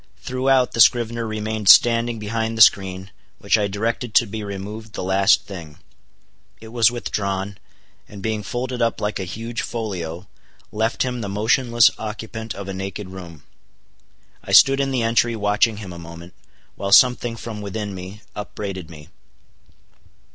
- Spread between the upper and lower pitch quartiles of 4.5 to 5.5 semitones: No, average, 3.0 semitones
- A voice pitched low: Yes, low, 105 Hz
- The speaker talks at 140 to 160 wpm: Yes, average, 155 wpm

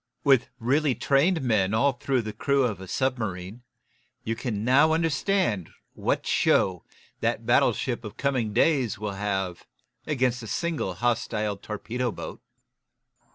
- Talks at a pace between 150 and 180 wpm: No, slow, 135 wpm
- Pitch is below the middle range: Yes, low, 120 Hz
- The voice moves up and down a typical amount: Yes, average, 4.8 semitones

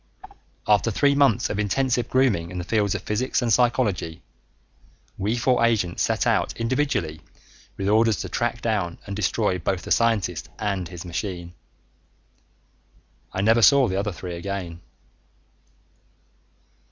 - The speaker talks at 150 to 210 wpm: No, average, 140 wpm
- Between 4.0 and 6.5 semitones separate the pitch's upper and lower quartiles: Yes, average, 4.5 semitones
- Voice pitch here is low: Yes, low, 105 Hz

